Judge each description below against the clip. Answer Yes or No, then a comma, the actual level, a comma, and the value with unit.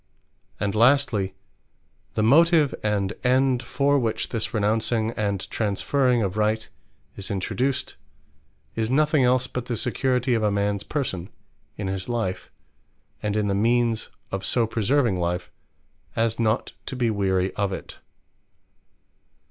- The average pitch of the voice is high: No, low, 110 Hz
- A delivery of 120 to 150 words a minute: Yes, slow, 135 wpm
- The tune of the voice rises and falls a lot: No, average, 3.9 semitones